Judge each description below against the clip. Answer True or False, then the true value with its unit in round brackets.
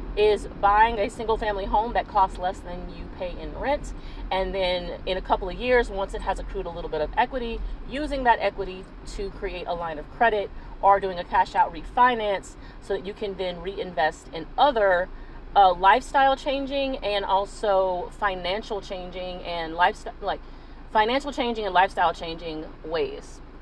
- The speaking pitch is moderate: False (195 Hz)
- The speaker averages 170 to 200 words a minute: True (175 wpm)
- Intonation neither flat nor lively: True (3.7 semitones)